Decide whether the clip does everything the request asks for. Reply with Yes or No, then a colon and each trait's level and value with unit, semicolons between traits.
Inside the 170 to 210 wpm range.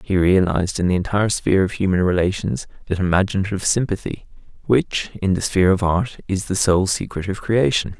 Yes: average, 180 wpm